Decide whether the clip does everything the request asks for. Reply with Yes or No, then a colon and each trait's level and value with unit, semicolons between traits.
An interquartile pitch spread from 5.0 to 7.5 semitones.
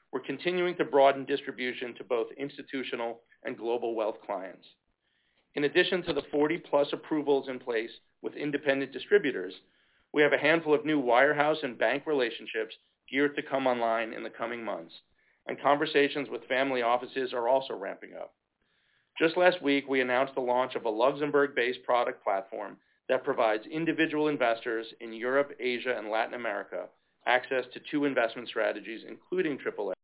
No: average, 3.3 semitones